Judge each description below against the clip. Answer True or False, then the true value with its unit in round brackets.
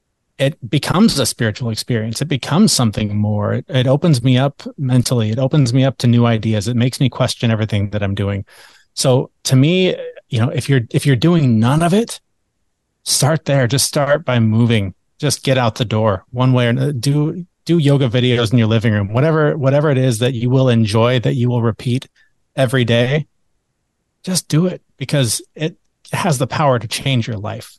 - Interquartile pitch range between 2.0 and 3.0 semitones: False (3.7 semitones)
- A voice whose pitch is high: False (130 Hz)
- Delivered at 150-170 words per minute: False (200 wpm)